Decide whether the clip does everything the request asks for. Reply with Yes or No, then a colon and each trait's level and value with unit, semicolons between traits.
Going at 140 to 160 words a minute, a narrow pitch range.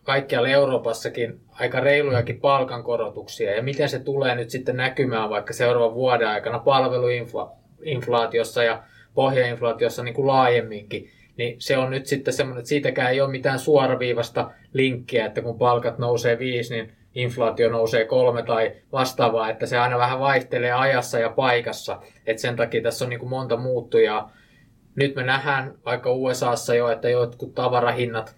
Yes: average, 150 wpm; narrow, 2.1 semitones